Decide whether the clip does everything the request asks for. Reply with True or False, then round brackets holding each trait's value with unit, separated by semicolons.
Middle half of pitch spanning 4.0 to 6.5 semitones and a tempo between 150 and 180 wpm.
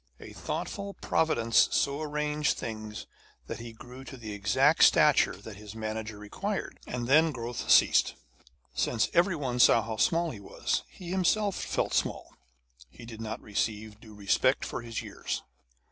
True (5.6 semitones; 160 wpm)